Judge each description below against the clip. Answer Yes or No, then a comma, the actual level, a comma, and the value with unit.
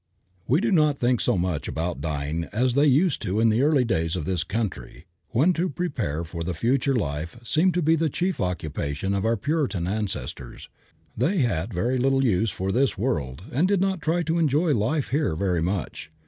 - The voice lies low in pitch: Yes, low, 115 Hz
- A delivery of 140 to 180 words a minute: No, average, 200 wpm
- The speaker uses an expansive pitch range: Yes, wide, 9.0 semitones